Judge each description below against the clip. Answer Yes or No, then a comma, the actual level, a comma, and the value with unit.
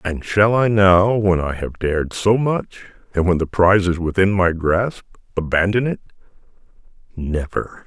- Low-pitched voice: Yes, very low, 95 Hz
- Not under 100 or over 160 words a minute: Yes, average, 150 wpm